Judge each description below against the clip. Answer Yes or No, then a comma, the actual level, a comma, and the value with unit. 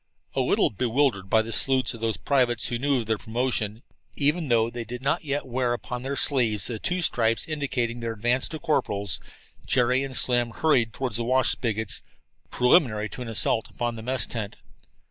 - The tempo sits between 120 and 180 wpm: No, average, 190 wpm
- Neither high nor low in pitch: No, low, 120 Hz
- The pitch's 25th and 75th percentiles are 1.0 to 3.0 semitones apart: Yes, average, 2.7 semitones